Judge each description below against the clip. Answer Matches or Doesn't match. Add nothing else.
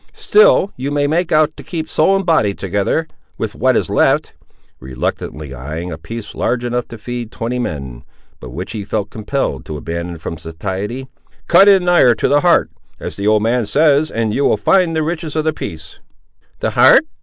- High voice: Doesn't match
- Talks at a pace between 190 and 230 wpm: Matches